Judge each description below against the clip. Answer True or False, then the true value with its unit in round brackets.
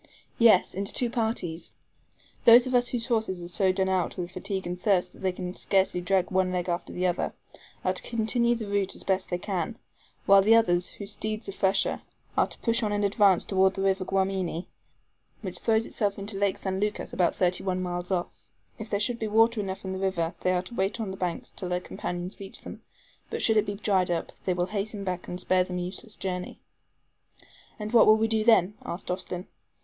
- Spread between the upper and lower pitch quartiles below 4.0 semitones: True (2.9 semitones)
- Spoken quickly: True (220 wpm)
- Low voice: False (195 Hz)